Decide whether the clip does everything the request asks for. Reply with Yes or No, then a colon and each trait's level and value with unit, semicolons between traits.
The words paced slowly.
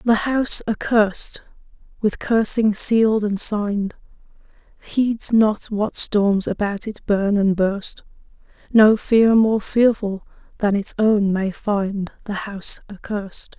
Yes: slow, 130 wpm